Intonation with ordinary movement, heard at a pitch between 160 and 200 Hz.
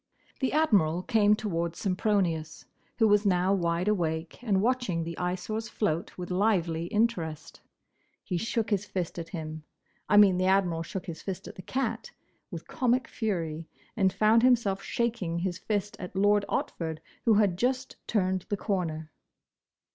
Yes: average, 4.2 semitones; high, 190 Hz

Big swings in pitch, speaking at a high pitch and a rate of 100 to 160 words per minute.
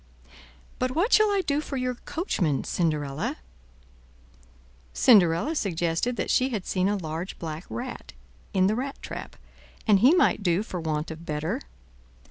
Yes: wide, 7.8 semitones; high, 195 Hz; average, 150 wpm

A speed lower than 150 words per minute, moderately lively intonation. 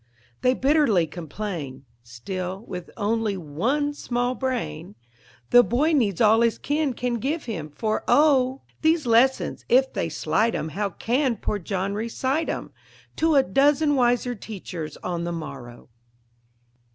No: average, 140 wpm; wide, 6.6 semitones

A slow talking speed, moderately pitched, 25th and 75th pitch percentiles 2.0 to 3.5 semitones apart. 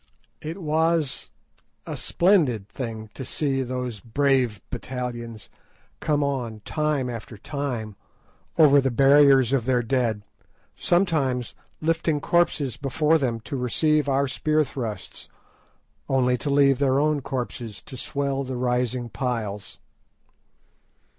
No: slow, 120 wpm; low, 130 Hz; average, 3.2 semitones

